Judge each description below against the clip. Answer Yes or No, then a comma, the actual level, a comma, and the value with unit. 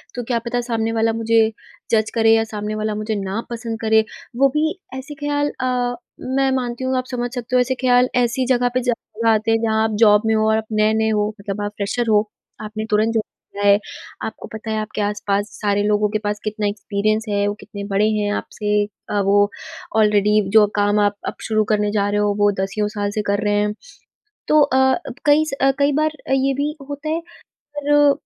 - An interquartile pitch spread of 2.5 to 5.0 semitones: Yes, average, 2.9 semitones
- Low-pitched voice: No, high, 220 Hz